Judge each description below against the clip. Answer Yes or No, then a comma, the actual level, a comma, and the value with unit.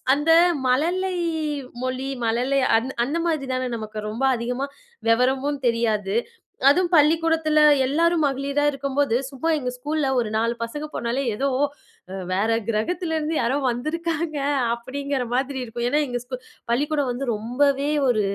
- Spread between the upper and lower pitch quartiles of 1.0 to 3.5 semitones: No, average, 4.0 semitones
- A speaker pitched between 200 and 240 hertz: No, very high, 270 Hz